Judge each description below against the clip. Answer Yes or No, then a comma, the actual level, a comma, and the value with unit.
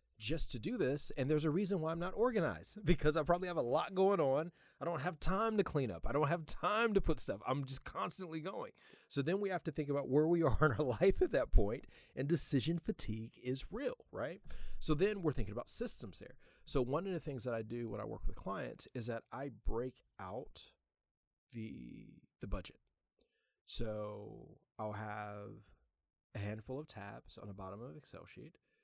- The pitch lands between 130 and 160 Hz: Yes, medium, 140 Hz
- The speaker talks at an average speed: No, fast, 210 wpm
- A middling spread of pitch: No, wide, 7.2 semitones